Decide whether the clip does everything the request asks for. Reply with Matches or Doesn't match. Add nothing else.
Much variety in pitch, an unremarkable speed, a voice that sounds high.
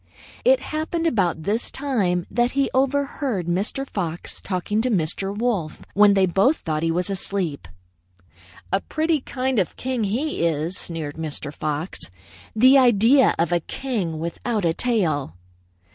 Matches